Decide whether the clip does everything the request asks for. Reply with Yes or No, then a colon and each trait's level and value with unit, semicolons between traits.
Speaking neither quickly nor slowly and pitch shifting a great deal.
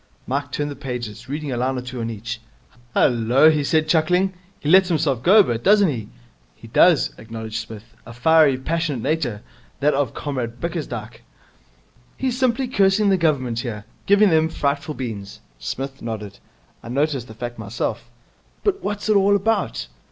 Yes: average, 170 wpm; wide, 6.2 semitones